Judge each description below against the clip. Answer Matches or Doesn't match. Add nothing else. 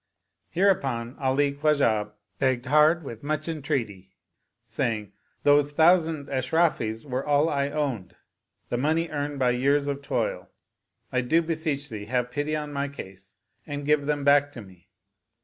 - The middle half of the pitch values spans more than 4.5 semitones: Doesn't match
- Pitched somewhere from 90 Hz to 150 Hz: Matches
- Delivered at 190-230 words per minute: Doesn't match